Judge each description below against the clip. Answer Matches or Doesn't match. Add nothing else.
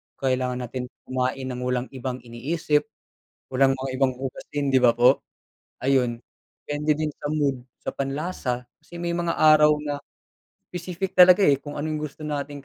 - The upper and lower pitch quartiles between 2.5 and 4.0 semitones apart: Matches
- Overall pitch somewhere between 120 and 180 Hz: Matches